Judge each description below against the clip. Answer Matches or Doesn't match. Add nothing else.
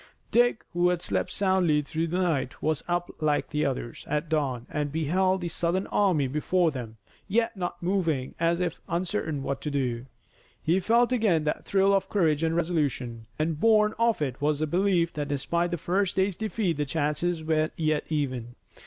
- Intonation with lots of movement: Doesn't match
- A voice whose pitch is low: Doesn't match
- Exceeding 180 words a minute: Matches